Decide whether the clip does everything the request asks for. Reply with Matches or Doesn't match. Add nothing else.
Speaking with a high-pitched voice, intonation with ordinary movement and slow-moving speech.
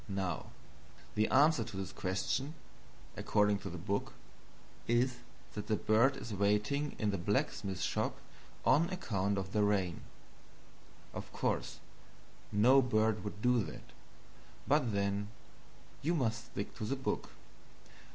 Doesn't match